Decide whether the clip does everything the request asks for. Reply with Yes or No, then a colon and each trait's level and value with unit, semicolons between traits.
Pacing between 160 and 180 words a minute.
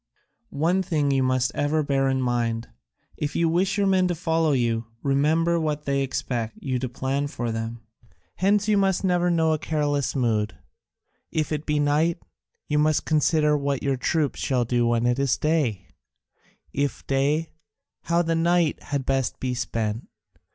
Yes: average, 170 wpm